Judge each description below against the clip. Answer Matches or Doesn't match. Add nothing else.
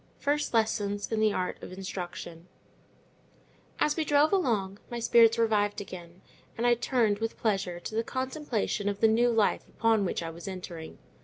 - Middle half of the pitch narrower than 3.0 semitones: Doesn't match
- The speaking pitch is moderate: Doesn't match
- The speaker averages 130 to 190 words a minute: Matches